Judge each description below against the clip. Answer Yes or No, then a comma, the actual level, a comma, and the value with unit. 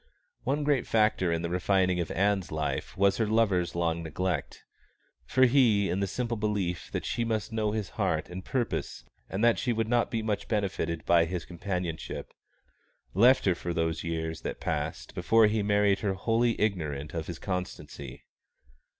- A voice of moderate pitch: No, very low, 95 Hz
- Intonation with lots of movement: No, average, 4.5 semitones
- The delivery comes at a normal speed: Yes, average, 175 wpm